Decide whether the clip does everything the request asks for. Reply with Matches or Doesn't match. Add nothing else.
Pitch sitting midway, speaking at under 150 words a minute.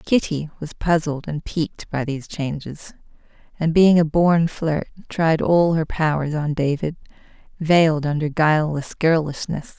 Matches